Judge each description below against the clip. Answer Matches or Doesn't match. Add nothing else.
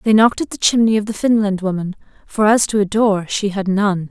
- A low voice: Doesn't match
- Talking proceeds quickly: Matches